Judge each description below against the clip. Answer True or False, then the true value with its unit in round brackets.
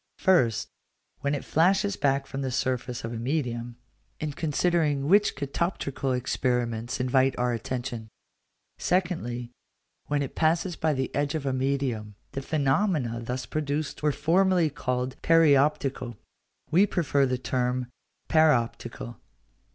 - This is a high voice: False (135 Hz)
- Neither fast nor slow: False (130 wpm)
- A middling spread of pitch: True (3.9 semitones)